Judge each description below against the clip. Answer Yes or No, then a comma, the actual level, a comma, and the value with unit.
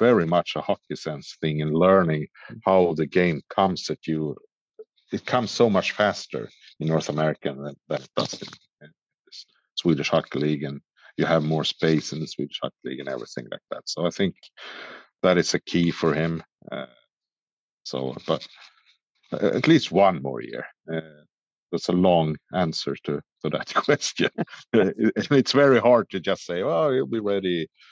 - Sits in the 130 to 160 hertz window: No, very low, 80 Hz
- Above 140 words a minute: Yes, average, 175 wpm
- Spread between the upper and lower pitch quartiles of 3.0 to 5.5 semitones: Yes, average, 3.7 semitones